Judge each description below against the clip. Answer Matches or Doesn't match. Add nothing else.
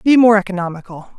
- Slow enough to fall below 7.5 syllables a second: Matches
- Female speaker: Matches